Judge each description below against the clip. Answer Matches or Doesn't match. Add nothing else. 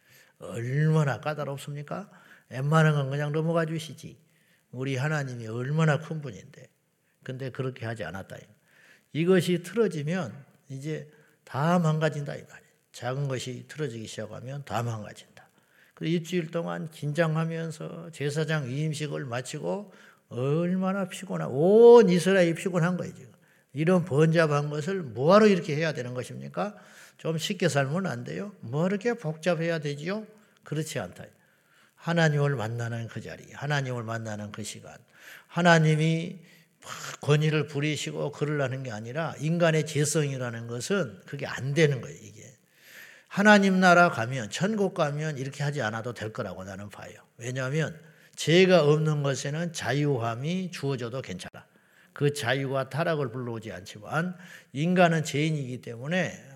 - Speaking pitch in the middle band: Matches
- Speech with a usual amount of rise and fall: Matches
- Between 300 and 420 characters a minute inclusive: Matches